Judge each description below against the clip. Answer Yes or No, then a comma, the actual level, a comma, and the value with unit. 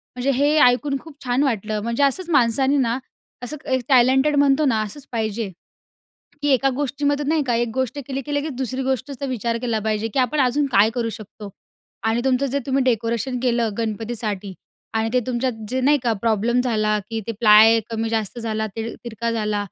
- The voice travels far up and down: No, average, 3.4 semitones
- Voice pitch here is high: Yes, high, 245 Hz